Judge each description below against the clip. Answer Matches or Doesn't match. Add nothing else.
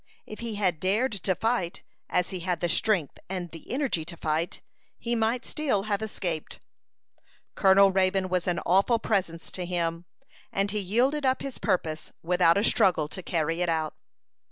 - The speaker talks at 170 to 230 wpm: Matches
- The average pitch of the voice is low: Doesn't match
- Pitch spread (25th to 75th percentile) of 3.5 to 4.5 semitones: Matches